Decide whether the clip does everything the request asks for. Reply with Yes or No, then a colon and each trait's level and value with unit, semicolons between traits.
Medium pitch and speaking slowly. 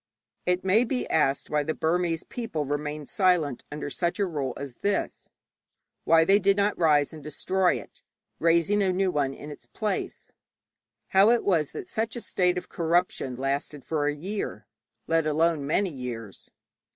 No: medium, 165 Hz; average, 175 wpm